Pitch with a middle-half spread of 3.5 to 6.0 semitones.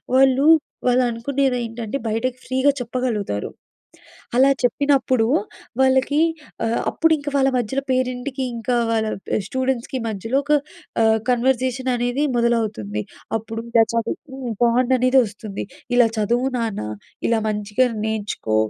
No: average, 2.7 semitones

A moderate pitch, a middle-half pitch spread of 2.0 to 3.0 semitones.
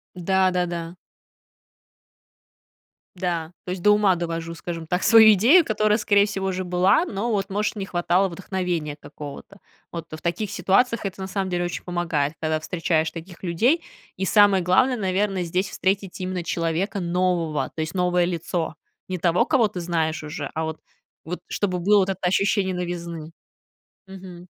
Yes: medium, 180 Hz; narrow, 2.5 semitones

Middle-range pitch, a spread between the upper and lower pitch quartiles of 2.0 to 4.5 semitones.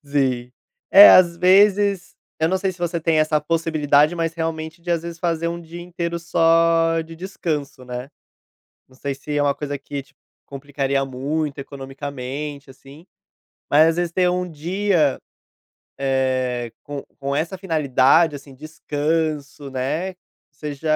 Yes: medium, 155 Hz; average, 3.3 semitones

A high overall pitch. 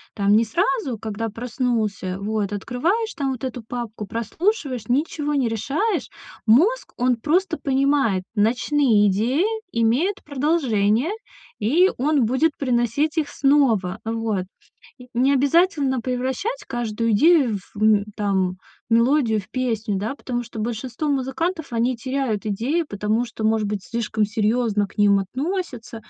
Yes: high, 240 Hz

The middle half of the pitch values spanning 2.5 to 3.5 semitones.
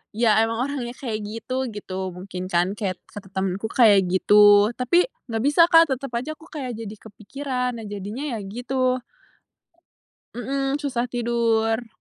No: average, 4.0 semitones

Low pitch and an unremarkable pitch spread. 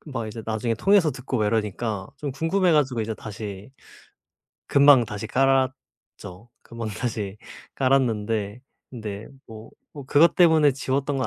Yes: low, 120 Hz; average, 4.3 semitones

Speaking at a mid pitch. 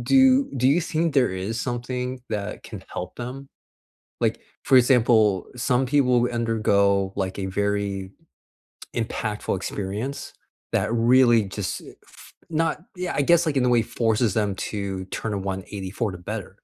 No: low, 115 Hz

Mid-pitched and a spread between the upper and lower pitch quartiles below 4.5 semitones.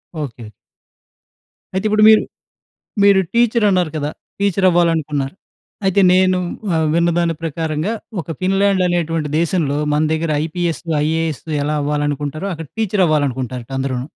Yes: medium, 165 Hz; average, 3.9 semitones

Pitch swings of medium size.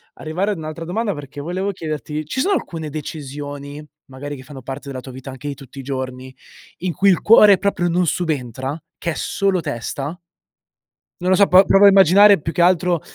Yes: average, 4.8 semitones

